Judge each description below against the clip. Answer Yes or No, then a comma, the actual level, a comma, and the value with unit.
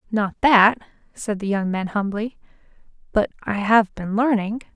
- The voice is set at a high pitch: Yes, high, 210 Hz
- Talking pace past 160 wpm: No, average, 150 wpm